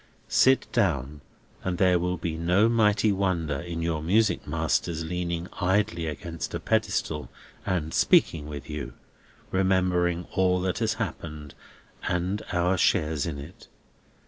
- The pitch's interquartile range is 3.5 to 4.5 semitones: No, average, 2.7 semitones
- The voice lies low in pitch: Yes, very low, 85 Hz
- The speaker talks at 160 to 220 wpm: No, slow, 135 wpm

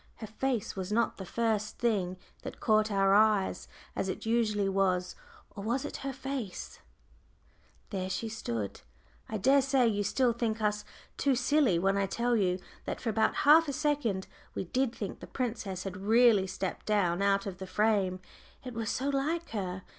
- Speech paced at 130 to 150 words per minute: No, average, 170 wpm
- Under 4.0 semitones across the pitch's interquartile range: No, average, 4.3 semitones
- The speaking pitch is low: No, high, 215 Hz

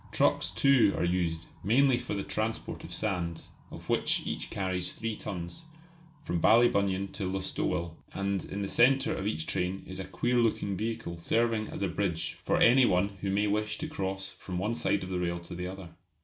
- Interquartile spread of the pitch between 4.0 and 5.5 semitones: No, average, 3.6 semitones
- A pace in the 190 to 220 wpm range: Yes, average, 195 wpm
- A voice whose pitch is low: Yes, low, 100 Hz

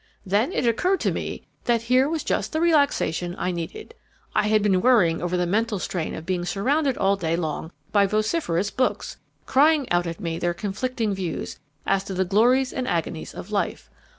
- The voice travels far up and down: Yes, wide, 6.4 semitones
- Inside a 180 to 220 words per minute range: Yes, average, 190 wpm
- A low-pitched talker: No, high, 205 Hz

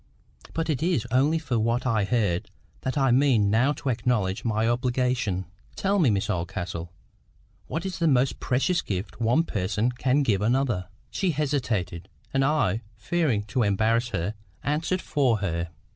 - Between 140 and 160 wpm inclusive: Yes, average, 155 wpm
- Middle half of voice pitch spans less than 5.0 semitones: No, average, 5.3 semitones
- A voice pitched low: Yes, low, 120 Hz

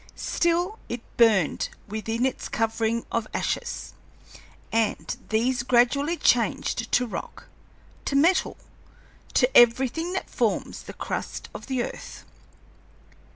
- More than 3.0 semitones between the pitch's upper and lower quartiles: Yes, average, 3.7 semitones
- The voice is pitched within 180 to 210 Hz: No, high, 240 Hz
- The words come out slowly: Yes, slow, 110 wpm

